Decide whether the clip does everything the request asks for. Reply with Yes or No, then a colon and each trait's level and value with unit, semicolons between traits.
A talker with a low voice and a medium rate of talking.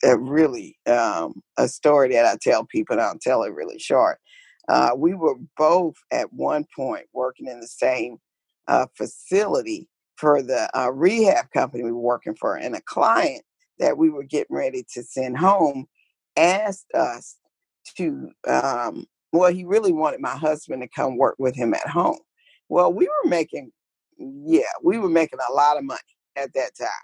No: high, 210 Hz; average, 180 wpm